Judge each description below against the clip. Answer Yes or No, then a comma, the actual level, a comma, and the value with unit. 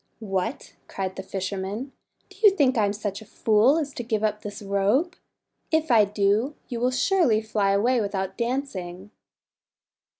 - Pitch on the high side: Yes, high, 215 Hz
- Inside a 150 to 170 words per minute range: Yes, average, 165 wpm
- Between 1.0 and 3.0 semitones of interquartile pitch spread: No, average, 4.4 semitones